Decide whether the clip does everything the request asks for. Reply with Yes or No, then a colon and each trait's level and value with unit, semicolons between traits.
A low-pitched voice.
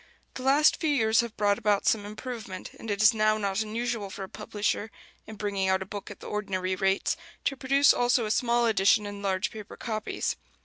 No: high, 215 Hz